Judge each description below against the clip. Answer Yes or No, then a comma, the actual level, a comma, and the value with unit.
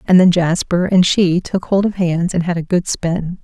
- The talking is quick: Yes, fast, 245 wpm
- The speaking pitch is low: No, medium, 180 Hz